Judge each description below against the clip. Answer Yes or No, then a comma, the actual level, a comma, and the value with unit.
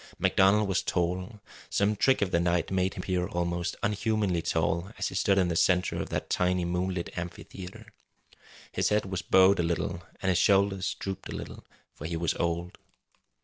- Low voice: Yes, very low, 90 Hz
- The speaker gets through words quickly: No, average, 185 wpm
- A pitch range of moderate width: No, narrow, 2.1 semitones